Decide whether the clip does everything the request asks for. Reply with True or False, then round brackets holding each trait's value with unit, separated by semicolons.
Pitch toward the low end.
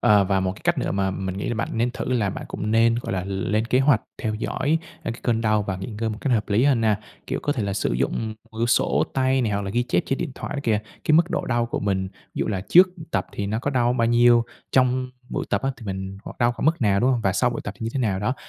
True (115 Hz)